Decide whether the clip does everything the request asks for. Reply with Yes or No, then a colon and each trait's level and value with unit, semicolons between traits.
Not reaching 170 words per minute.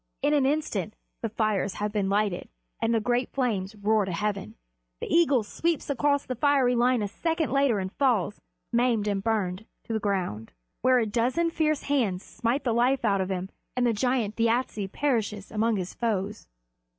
No: average, 185 wpm